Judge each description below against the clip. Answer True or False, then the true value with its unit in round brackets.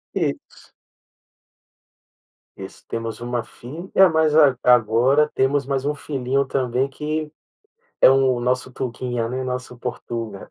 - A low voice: True (130 Hz)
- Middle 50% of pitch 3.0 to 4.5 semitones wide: False (2.6 semitones)